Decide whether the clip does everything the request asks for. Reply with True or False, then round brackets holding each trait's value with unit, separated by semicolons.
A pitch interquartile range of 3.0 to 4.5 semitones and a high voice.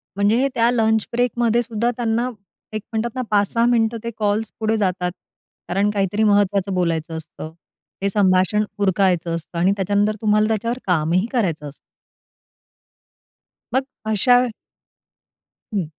True (3.3 semitones; 205 Hz)